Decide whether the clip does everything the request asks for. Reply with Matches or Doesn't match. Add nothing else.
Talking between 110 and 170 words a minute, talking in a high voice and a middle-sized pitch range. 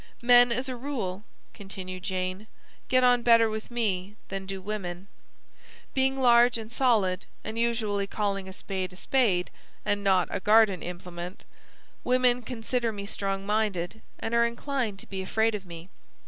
Matches